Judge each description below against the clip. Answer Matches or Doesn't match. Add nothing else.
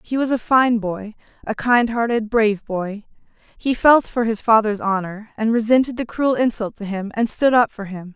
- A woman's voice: Matches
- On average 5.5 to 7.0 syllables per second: Doesn't match